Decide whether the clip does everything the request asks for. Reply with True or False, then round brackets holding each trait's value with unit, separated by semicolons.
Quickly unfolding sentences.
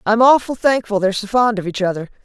True (240 wpm)